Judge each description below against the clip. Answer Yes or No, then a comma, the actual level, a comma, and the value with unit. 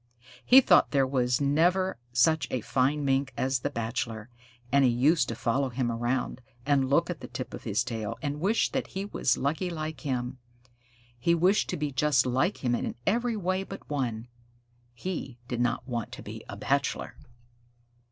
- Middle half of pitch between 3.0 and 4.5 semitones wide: No, average, 4.9 semitones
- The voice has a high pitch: No, low, 135 Hz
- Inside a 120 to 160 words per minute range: No, average, 180 wpm